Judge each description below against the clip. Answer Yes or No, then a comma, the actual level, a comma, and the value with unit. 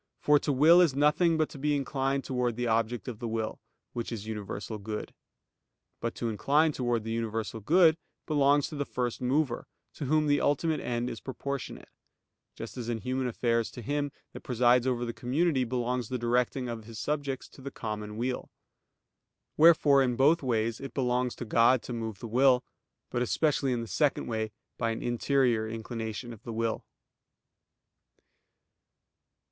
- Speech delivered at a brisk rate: No, average, 175 wpm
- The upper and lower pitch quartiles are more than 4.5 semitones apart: No, average, 3.4 semitones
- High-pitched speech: No, low, 125 Hz